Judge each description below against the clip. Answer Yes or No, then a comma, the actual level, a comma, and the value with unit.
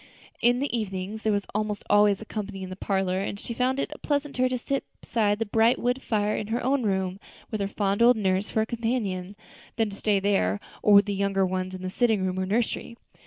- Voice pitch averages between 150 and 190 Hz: No, high, 205 Hz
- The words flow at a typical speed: No, fast, 225 wpm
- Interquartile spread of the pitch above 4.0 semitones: No, average, 3.3 semitones